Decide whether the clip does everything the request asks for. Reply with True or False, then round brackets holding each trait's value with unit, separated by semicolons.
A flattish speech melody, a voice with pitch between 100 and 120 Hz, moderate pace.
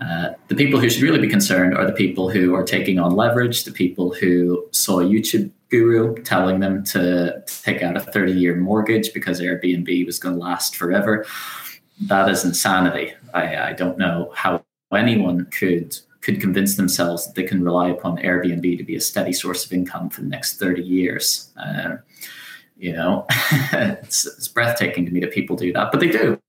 False (1.7 semitones; 90 Hz; 190 wpm)